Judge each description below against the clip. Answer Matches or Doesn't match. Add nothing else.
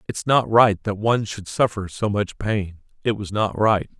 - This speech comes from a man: Matches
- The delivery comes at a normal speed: Doesn't match